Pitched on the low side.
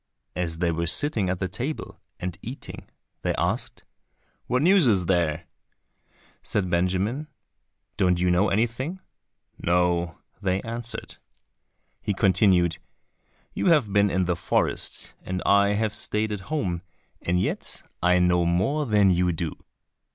Yes: very low, 95 Hz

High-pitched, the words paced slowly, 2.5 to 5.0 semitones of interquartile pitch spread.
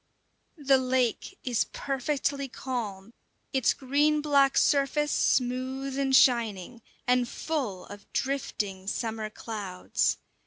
Yes: very high, 255 Hz; slow, 105 wpm; average, 3.7 semitones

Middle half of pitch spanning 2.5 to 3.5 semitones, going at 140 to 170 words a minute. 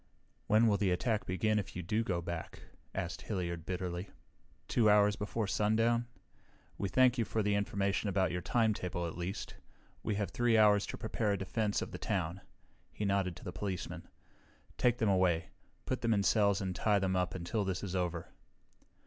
No: average, 3.0 semitones; average, 185 wpm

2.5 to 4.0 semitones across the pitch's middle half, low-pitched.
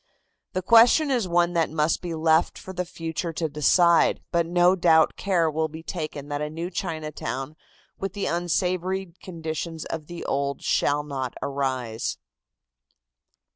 No: average, 2.8 semitones; medium, 165 Hz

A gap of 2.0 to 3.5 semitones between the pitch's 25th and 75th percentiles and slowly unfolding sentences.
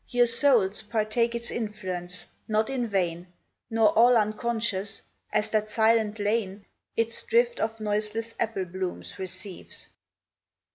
Yes: narrow, 2.6 semitones; slow, 125 wpm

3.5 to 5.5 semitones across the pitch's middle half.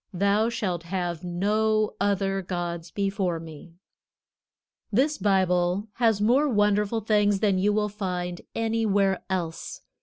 No: average, 3.0 semitones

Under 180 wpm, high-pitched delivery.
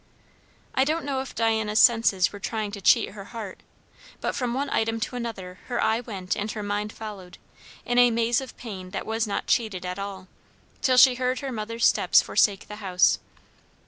No: average, 195 wpm; high, 220 Hz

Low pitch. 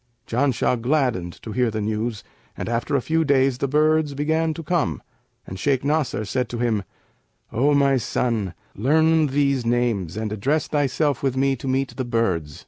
Yes: low, 130 Hz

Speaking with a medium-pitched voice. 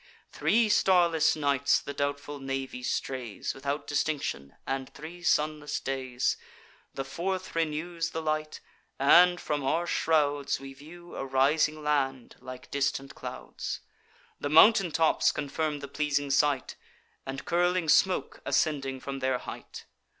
Yes: medium, 145 Hz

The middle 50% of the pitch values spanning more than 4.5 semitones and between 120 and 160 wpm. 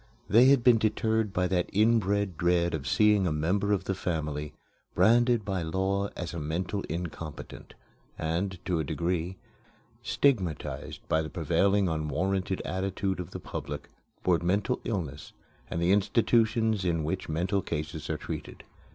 No: average, 3.7 semitones; average, 150 wpm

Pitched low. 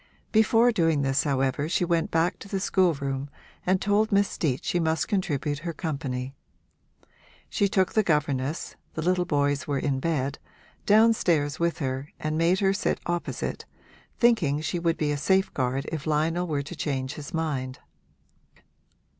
No: medium, 160 Hz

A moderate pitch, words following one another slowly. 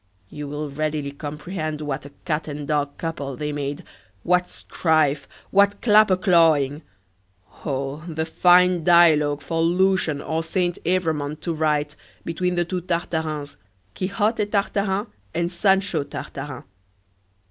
Yes: medium, 160 Hz; slow, 125 wpm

